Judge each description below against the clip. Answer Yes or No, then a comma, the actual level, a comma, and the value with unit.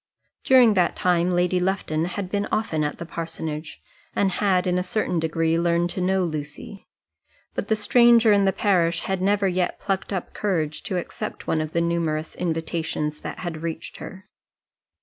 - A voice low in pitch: No, medium, 180 Hz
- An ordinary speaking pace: Yes, average, 175 wpm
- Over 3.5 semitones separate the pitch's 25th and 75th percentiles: No, average, 2.9 semitones